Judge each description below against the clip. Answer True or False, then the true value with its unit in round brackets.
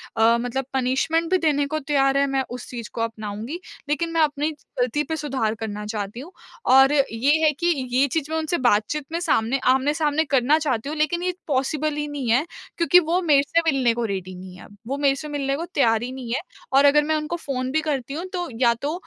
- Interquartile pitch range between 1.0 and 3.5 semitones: False (4.0 semitones)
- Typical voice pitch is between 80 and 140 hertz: False (280 Hz)